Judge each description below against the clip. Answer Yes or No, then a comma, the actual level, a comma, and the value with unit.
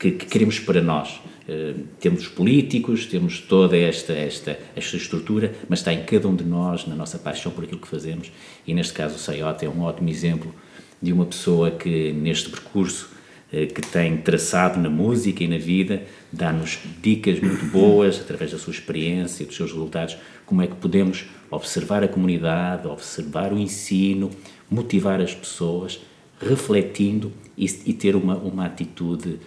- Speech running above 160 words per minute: Yes, average, 170 wpm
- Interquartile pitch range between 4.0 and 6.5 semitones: No, average, 2.8 semitones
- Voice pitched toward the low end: Yes, very low, 90 Hz